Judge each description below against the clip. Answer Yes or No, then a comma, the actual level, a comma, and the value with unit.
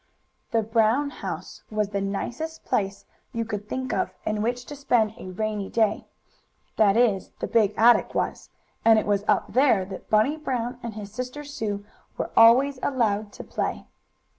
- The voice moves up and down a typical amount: Yes, average, 3.2 semitones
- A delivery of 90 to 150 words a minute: No, average, 170 wpm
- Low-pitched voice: No, high, 225 Hz